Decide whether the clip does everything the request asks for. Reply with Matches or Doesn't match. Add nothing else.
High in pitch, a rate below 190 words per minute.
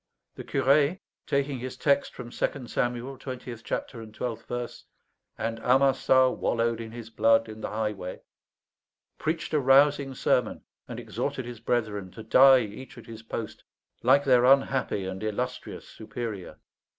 Doesn't match